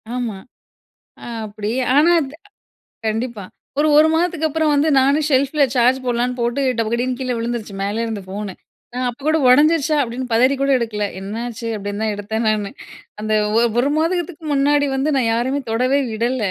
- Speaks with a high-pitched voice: Yes, very high, 250 Hz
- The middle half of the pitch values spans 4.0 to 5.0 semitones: Yes, average, 4.3 semitones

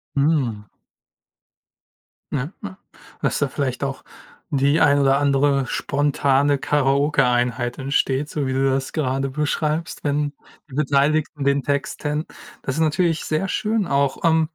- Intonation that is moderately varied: No, narrow, 2.0 semitones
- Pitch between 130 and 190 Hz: Yes, medium, 140 Hz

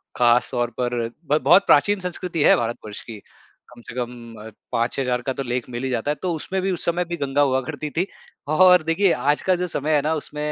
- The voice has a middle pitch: Yes, medium, 145 Hz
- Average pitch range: No, wide, 5.8 semitones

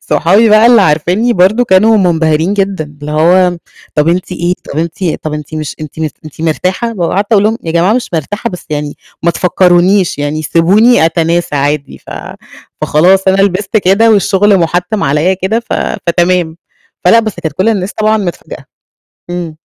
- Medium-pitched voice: Yes, medium, 180 Hz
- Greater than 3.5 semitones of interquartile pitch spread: Yes, average, 4.0 semitones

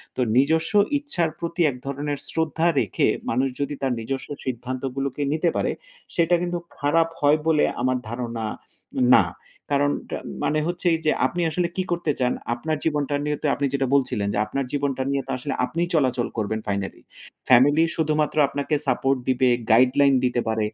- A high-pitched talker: No, medium, 140 Hz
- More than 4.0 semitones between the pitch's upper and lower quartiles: No, average, 3.7 semitones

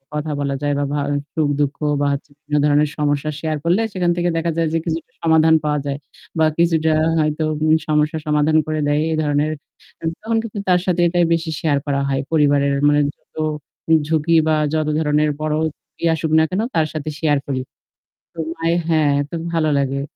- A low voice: No, medium, 155 Hz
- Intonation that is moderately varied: No, narrow, 2.0 semitones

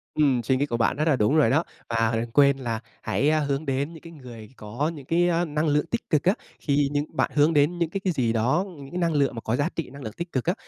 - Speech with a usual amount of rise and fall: Yes, average, 4.1 semitones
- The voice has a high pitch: No, medium, 145 Hz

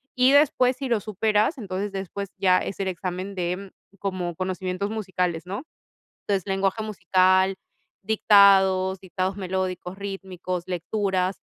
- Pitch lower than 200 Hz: Yes, high, 190 Hz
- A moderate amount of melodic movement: No, narrow, 1.6 semitones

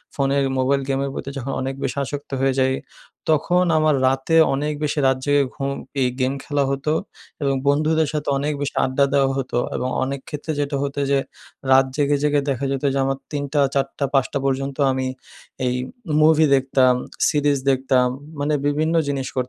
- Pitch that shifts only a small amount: Yes, narrow, 1.5 semitones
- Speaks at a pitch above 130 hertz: Yes, medium, 140 Hz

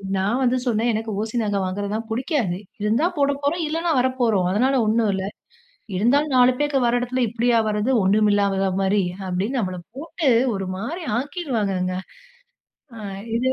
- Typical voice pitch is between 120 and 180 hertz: No, high, 230 Hz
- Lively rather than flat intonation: No, average, 4.6 semitones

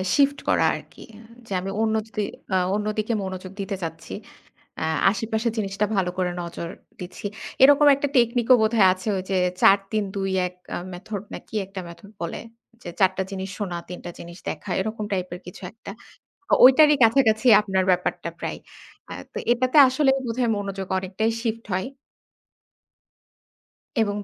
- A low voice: No, high, 200 Hz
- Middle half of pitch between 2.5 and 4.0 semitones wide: Yes, average, 3.3 semitones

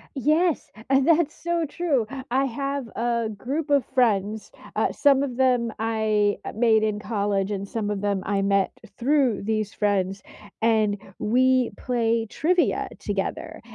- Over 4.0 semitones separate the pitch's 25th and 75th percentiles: Yes, average, 4.7 semitones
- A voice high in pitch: Yes, high, 230 Hz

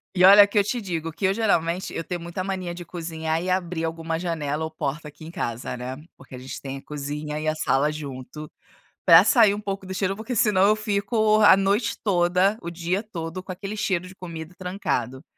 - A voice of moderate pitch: Yes, medium, 175 Hz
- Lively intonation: No, average, 3.8 semitones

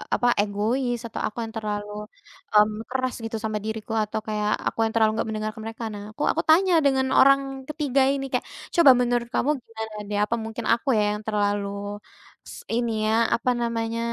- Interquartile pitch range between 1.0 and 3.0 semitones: Yes, narrow, 2.4 semitones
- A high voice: Yes, high, 225 Hz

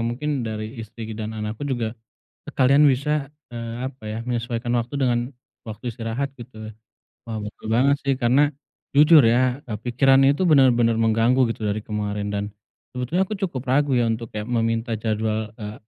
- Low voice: Yes, low, 120 Hz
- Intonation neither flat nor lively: Yes, average, 3.4 semitones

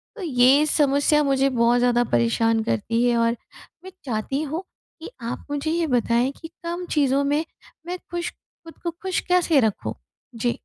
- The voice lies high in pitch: Yes, very high, 275 Hz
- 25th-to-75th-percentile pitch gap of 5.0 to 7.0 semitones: Yes, wide, 5.4 semitones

